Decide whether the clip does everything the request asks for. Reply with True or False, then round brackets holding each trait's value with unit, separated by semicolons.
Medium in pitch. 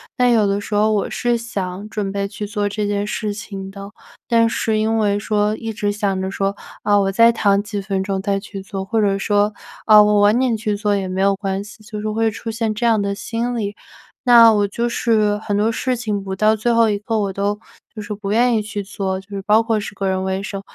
False (210 Hz)